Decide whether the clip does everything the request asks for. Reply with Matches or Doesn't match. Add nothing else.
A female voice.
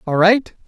Doesn't match